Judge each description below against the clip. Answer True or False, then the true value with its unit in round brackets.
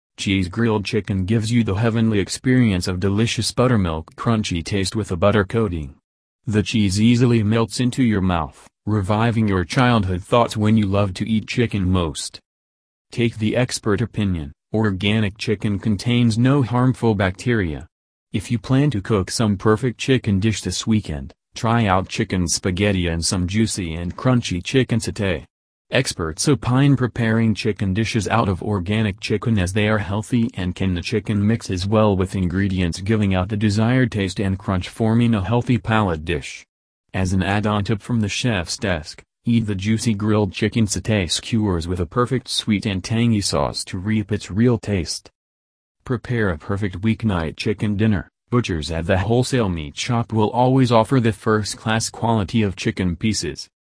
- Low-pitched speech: True (105 Hz)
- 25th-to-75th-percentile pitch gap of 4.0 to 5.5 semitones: False (3.5 semitones)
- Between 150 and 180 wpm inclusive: True (165 wpm)